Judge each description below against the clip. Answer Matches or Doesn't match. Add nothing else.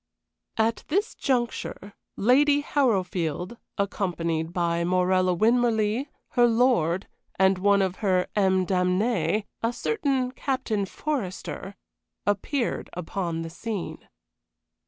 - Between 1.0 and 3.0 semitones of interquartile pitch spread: Doesn't match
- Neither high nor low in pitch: Doesn't match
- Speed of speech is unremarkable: Doesn't match